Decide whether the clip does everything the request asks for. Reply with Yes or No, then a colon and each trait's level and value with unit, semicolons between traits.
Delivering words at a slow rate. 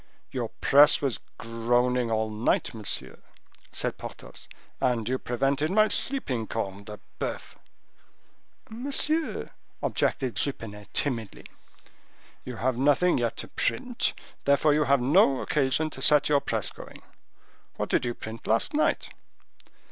Yes: slow, 130 wpm